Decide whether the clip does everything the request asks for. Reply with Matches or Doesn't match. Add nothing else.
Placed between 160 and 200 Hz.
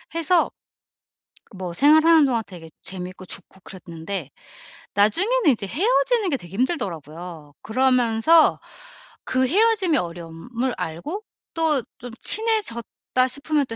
Doesn't match